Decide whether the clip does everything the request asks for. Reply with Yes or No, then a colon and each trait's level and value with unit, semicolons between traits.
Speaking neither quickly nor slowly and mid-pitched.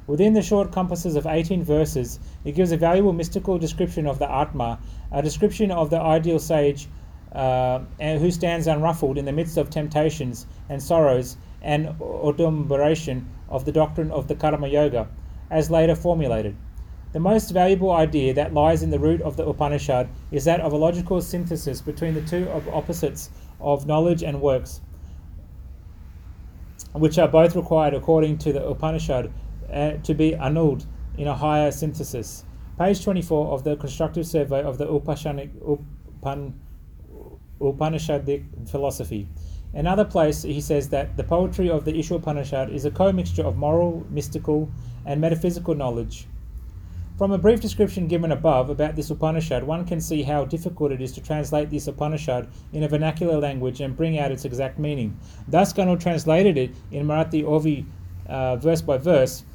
Yes: average, 160 wpm; medium, 150 Hz